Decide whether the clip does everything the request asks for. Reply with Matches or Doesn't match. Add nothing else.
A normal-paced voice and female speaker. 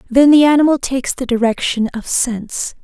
Matches